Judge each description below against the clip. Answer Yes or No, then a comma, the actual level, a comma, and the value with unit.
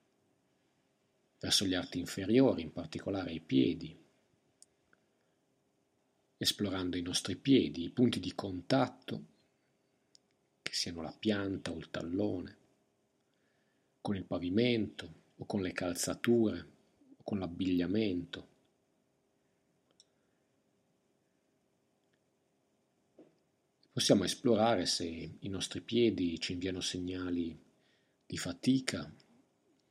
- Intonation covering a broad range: No, average, 3.4 semitones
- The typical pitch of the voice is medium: No, very low, 95 Hz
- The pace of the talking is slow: Yes, slow, 90 wpm